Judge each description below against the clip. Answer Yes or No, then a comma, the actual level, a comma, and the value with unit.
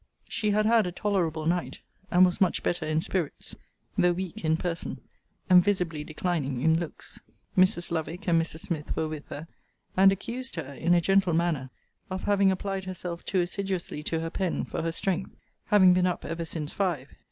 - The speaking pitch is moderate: Yes, medium, 175 Hz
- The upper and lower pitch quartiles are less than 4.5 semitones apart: Yes, average, 2.7 semitones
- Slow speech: No, average, 185 wpm